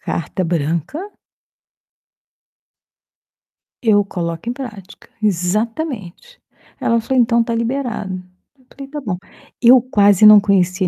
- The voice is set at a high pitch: Yes, high, 215 Hz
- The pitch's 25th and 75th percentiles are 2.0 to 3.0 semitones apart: No, average, 5.0 semitones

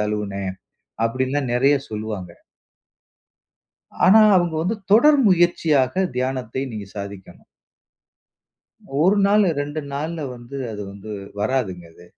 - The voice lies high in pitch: No, low, 130 Hz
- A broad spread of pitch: Yes, wide, 7.8 semitones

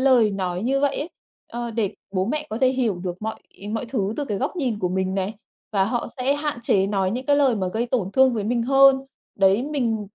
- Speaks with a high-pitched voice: Yes, high, 230 Hz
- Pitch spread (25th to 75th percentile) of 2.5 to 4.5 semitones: No, average, 5.2 semitones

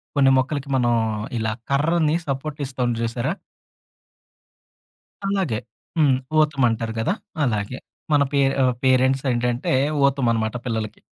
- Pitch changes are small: No, average, 3.2 semitones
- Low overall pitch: Yes, low, 130 Hz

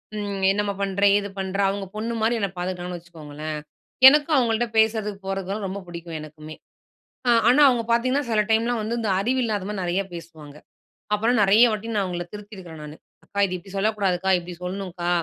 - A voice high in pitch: Yes, high, 195 Hz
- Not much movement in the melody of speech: No, average, 3.7 semitones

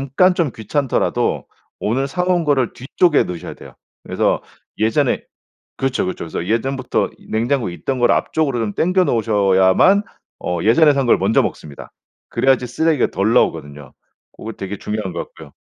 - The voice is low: Yes, low, 120 Hz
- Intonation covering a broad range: Yes, wide, 5.9 semitones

